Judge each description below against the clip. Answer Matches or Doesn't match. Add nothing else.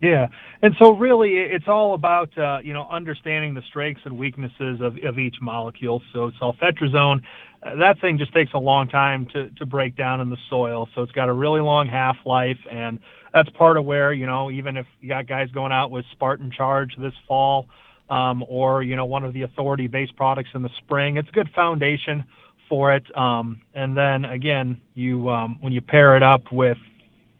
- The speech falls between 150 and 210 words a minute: Matches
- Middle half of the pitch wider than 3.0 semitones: Doesn't match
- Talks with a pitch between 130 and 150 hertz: Matches